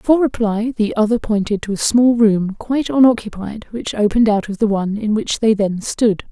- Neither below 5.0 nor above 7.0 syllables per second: Yes, 5.2 syllables/s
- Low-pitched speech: No, high, 220 Hz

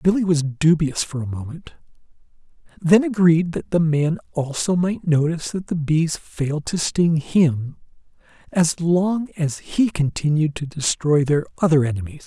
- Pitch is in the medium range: Yes, medium, 160 Hz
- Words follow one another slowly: No, average, 150 wpm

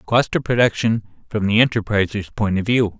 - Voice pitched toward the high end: No, low, 105 Hz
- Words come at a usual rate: Yes, average, 180 wpm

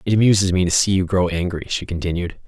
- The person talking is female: No, male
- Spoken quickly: Yes, fast, 240 wpm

